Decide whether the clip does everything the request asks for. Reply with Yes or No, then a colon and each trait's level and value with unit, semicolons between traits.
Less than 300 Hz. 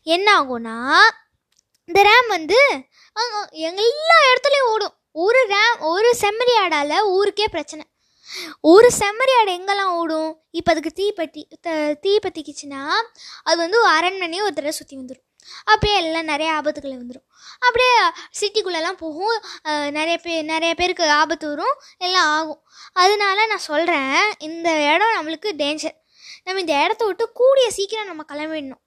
No: very high, 345 Hz